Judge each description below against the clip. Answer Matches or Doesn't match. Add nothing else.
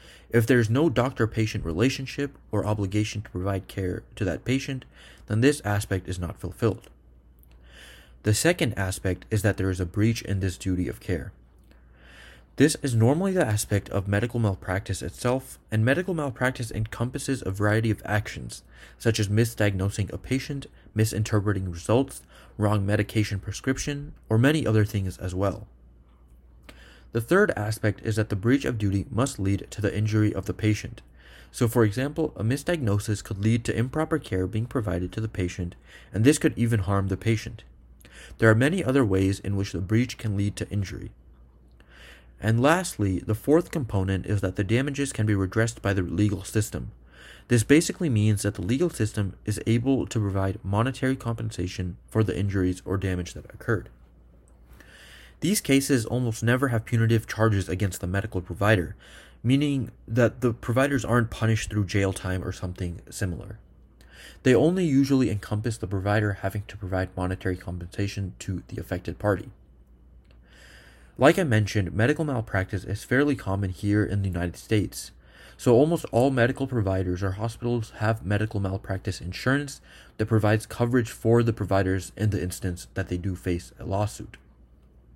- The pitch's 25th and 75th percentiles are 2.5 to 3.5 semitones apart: Doesn't match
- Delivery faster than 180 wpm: Doesn't match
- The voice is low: Matches